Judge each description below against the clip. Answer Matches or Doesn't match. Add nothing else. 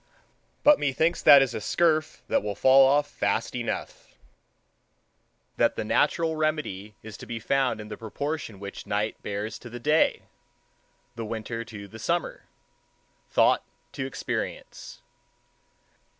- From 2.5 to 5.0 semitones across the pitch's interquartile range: Doesn't match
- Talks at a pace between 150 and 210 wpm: Doesn't match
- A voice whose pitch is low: Matches